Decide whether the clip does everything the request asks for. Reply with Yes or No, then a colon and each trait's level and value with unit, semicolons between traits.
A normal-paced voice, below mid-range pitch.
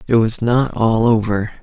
Yes: average, 185 wpm; low, 115 Hz